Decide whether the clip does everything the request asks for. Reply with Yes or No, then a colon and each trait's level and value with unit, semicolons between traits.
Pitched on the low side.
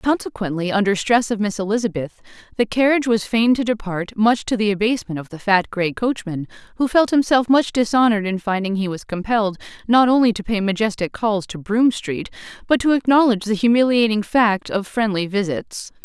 No: high, 215 Hz